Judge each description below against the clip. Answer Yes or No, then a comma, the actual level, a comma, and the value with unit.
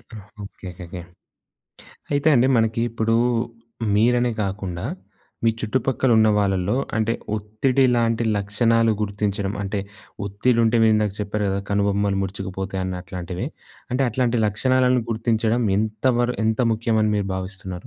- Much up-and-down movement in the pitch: No, average, 2.8 semitones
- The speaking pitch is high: No, low, 110 Hz